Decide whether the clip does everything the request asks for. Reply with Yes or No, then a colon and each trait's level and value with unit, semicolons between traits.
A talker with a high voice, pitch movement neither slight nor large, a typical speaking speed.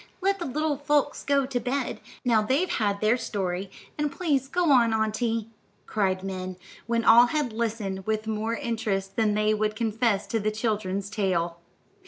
Yes: high, 220 Hz; average, 3.6 semitones; average, 170 wpm